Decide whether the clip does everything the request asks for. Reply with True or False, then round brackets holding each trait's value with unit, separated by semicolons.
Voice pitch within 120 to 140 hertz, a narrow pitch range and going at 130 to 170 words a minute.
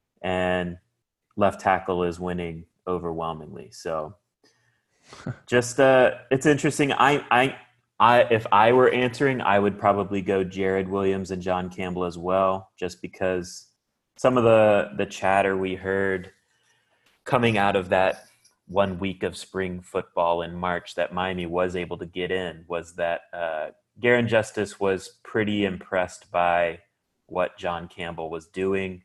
False (95 Hz; 2.0 semitones; 145 wpm)